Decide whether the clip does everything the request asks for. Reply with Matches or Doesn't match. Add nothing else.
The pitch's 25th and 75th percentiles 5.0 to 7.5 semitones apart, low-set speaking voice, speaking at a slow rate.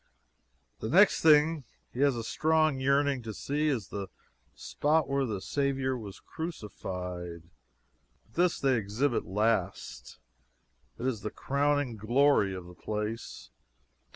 Matches